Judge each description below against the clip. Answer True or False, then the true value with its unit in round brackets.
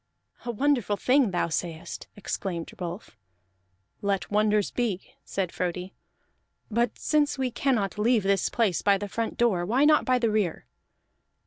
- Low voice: False (210 Hz)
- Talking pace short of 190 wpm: True (145 wpm)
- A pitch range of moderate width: True (4.2 semitones)